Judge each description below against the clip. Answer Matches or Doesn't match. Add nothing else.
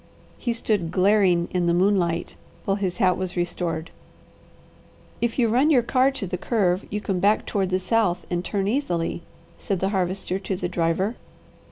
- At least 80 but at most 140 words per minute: Doesn't match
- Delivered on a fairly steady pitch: Doesn't match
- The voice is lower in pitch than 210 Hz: Matches